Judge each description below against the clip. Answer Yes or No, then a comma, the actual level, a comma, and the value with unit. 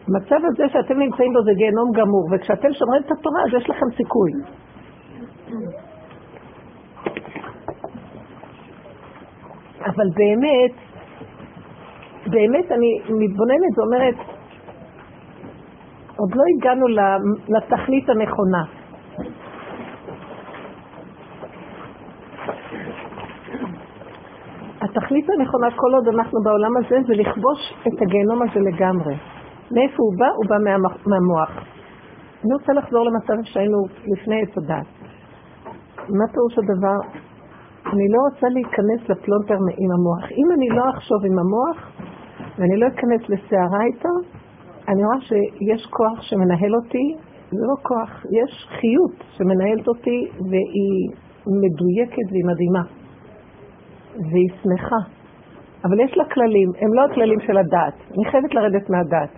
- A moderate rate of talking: Yes, average, 110 wpm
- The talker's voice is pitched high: Yes, high, 220 Hz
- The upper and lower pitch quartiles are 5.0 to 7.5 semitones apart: No, average, 4.1 semitones